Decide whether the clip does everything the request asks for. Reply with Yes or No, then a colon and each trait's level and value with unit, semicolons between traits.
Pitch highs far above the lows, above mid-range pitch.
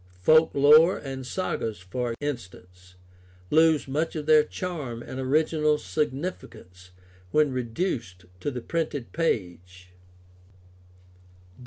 No: wide, 6.0 semitones; low, 135 Hz